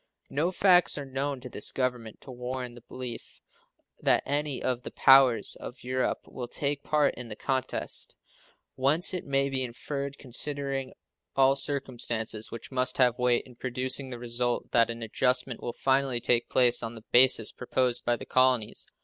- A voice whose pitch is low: Yes, low, 130 Hz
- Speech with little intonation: Yes, narrow, 2.1 semitones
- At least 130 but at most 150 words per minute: No, average, 170 wpm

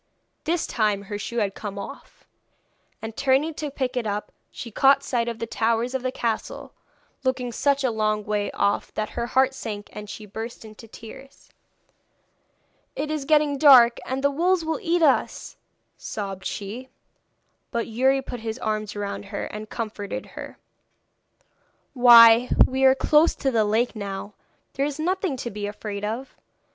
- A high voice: Yes, high, 235 Hz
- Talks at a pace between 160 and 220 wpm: Yes, average, 165 wpm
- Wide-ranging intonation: No, average, 4.1 semitones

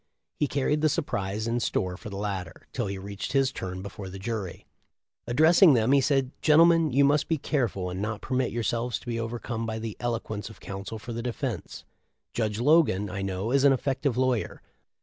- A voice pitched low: Yes, low, 115 Hz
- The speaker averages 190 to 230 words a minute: Yes, average, 195 wpm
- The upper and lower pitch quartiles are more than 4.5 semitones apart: Yes, average, 5.0 semitones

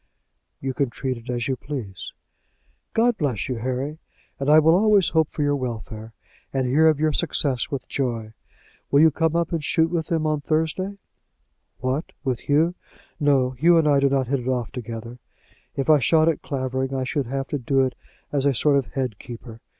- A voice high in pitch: No, medium, 140 Hz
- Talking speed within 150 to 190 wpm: No, average, 200 wpm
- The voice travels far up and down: No, average, 3.7 semitones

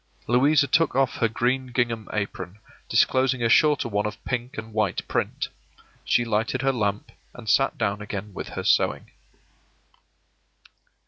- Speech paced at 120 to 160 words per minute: Yes, average, 145 wpm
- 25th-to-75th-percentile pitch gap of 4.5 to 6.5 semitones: No, average, 3.6 semitones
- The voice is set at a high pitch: No, low, 120 Hz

